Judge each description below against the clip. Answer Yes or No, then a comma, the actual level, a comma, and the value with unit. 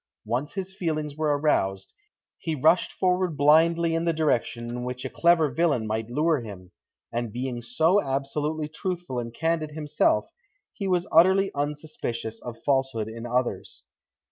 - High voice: No, medium, 150 Hz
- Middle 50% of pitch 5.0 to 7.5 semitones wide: Yes, average, 5.3 semitones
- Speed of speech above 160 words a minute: No, average, 150 wpm